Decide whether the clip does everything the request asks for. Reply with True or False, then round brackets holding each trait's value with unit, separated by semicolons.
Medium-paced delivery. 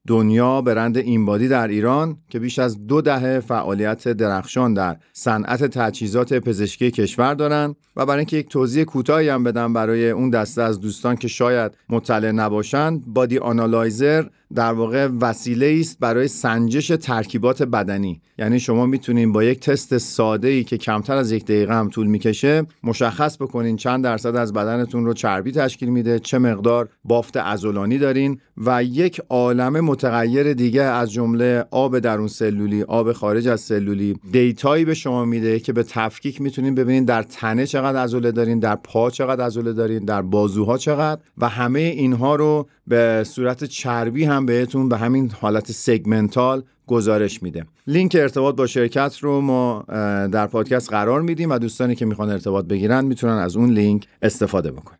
False (165 wpm)